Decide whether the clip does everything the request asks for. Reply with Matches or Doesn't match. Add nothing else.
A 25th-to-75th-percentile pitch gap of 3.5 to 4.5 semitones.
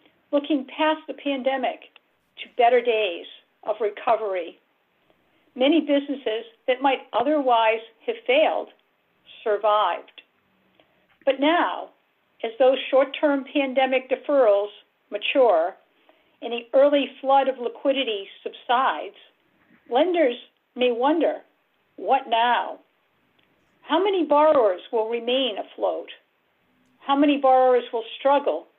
Matches